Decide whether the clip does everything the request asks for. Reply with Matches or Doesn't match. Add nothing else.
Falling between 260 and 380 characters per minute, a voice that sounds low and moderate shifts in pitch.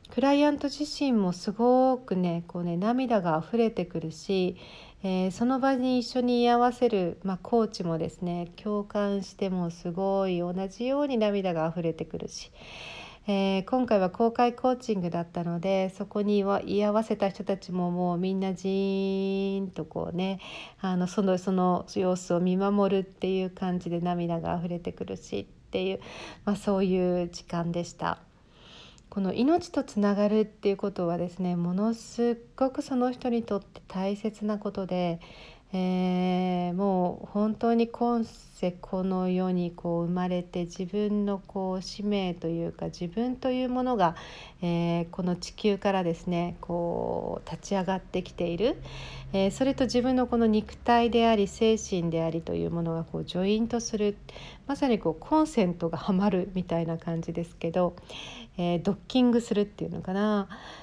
Doesn't match